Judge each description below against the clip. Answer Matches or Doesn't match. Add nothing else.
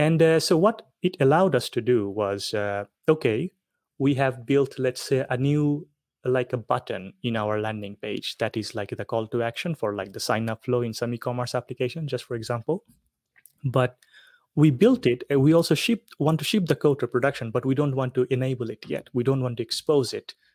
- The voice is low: Matches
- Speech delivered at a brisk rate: Matches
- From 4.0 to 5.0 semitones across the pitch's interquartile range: Matches